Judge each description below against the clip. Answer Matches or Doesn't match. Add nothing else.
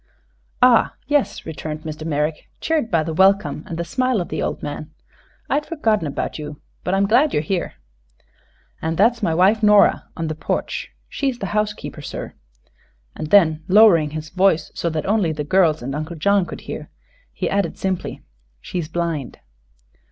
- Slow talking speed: Doesn't match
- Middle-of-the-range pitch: Matches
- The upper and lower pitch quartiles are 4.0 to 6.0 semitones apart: Matches